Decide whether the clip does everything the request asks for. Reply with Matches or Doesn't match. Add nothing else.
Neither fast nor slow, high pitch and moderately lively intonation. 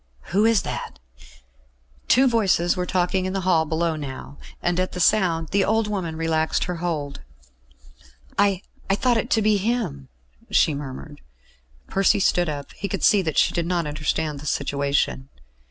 Doesn't match